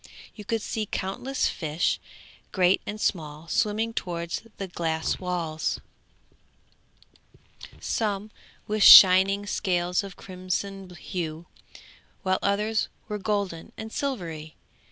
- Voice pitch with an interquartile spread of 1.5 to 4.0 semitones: Yes, average, 3.3 semitones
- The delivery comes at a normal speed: No, slow, 105 wpm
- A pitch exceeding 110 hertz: Yes, high, 190 Hz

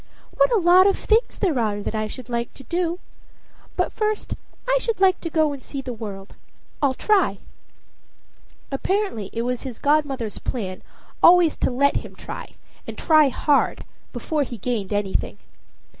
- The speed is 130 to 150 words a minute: No, average, 165 wpm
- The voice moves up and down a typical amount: No, wide, 7.5 semitones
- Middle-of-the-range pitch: No, very high, 280 Hz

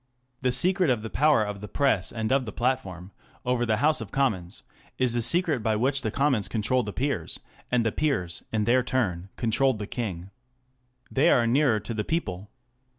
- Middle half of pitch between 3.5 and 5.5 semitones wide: Yes, average, 4.2 semitones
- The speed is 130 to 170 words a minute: No, average, 190 wpm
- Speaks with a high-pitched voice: No, low, 120 Hz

